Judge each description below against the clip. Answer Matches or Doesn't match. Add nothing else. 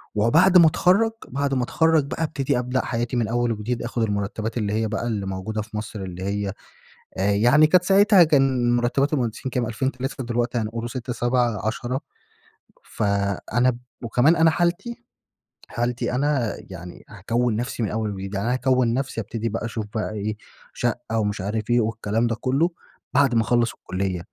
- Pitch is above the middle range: Doesn't match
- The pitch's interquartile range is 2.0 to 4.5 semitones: Matches